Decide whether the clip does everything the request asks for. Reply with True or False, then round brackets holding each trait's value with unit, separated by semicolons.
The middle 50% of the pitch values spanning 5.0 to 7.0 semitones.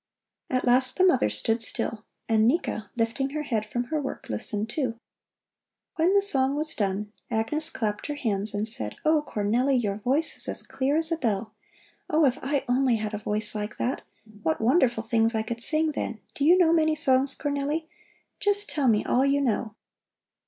True (5.3 semitones)